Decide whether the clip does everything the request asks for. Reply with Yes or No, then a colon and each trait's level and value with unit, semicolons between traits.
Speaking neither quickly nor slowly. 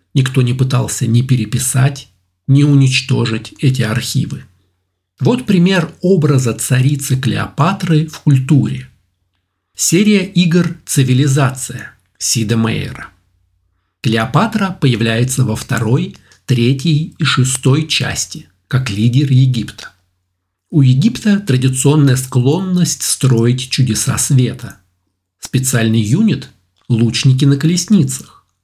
No: slow, 90 wpm